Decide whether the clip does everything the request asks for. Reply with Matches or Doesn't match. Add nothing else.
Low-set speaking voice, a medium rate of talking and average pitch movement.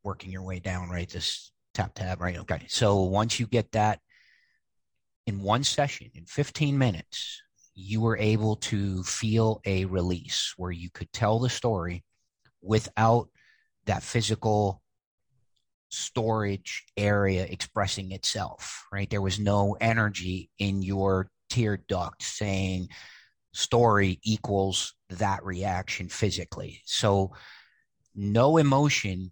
Doesn't match